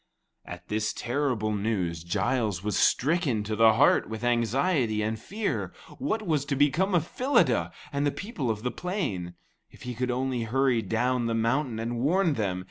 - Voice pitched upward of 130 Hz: No, low, 120 Hz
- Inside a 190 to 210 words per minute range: No, average, 175 wpm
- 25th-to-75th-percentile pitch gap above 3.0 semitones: Yes, average, 5.0 semitones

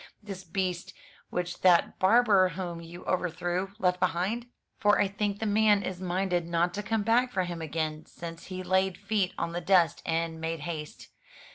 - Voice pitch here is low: No, medium, 185 Hz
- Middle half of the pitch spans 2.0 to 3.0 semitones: Yes, narrow, 2.6 semitones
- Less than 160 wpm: No, average, 175 wpm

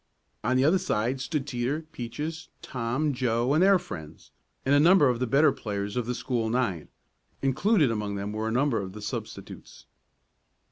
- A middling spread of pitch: Yes, average, 4.8 semitones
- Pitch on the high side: No, low, 125 Hz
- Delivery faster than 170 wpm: Yes, average, 180 wpm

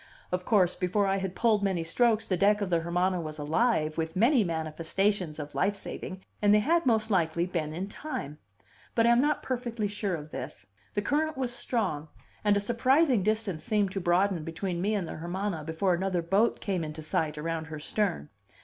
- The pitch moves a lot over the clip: No, average, 4.5 semitones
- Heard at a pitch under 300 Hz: Yes, high, 190 Hz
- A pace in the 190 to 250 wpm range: Yes, average, 200 wpm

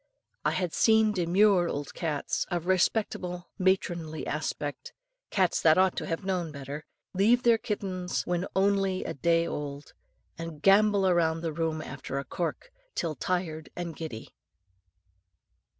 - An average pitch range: Yes, average, 3.3 semitones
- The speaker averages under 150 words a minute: Yes, average, 140 wpm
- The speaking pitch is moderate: Yes, medium, 175 Hz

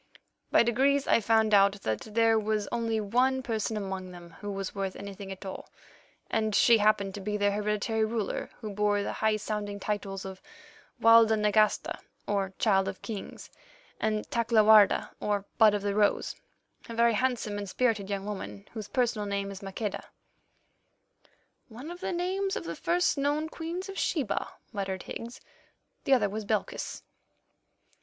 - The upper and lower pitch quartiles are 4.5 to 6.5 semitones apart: No, narrow, 2.5 semitones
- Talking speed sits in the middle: Yes, average, 165 wpm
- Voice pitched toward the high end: Yes, high, 215 Hz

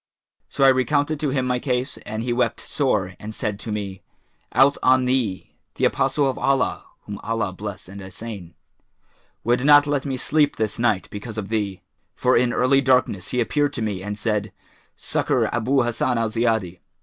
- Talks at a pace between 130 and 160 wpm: No, average, 185 wpm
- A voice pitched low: Yes, low, 120 Hz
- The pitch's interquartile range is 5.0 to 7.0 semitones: No, average, 4.0 semitones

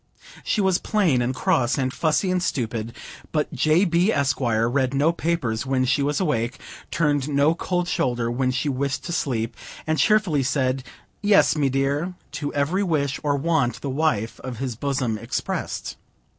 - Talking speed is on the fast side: No, average, 170 wpm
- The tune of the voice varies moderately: Yes, average, 4.1 semitones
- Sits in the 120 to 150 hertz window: Yes, medium, 140 Hz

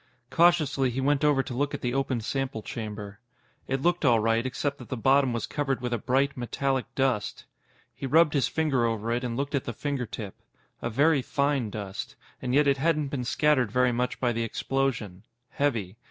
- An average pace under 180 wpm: No, average, 195 wpm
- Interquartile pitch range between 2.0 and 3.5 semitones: Yes, average, 3.2 semitones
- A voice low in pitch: Yes, low, 130 Hz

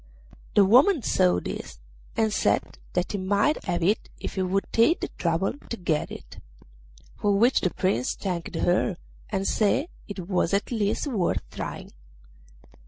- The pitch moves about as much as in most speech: Yes, average, 3.5 semitones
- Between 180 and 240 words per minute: No, average, 160 wpm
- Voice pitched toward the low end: No, high, 195 Hz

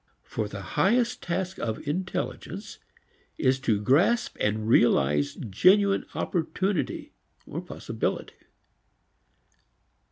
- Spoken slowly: Yes, slow, 85 wpm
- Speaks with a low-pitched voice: No, medium, 150 Hz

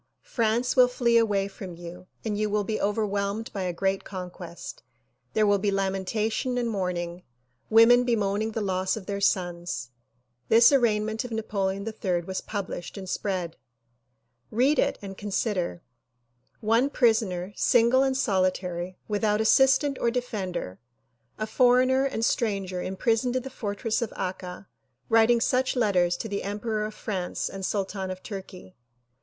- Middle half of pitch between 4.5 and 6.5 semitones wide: No, average, 3.4 semitones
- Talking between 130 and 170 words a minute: Yes, average, 150 wpm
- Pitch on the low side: No, high, 205 Hz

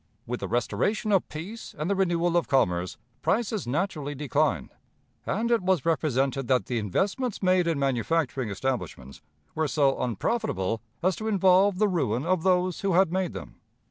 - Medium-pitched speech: Yes, medium, 165 Hz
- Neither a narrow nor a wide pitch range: No, wide, 6.3 semitones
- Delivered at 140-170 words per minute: Yes, average, 165 wpm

